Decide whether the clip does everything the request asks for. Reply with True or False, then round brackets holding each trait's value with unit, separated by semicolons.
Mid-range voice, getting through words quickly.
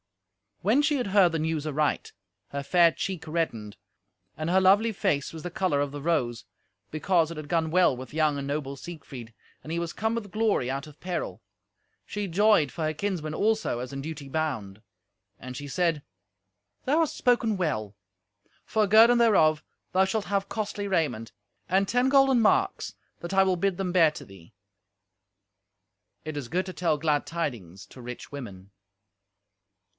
False (165 Hz; 175 wpm)